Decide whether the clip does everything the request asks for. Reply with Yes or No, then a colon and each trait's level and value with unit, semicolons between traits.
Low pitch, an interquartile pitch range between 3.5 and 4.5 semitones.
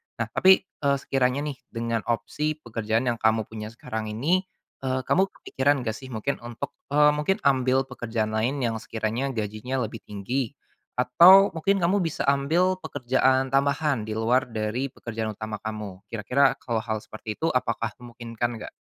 Yes: low, 125 Hz; average, 4.1 semitones